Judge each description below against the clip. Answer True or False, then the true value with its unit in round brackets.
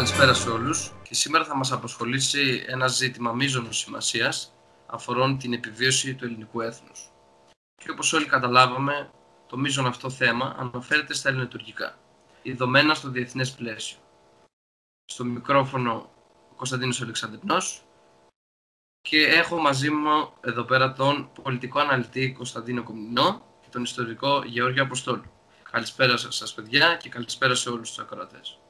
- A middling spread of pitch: True (3.5 semitones)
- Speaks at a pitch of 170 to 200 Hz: False (125 Hz)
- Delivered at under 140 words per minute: True (130 wpm)